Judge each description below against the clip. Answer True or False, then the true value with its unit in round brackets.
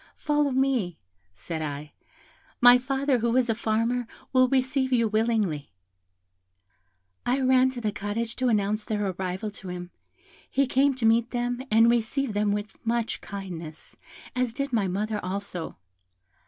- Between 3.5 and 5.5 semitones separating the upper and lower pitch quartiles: True (4.1 semitones)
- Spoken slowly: False (150 wpm)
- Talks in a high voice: True (225 Hz)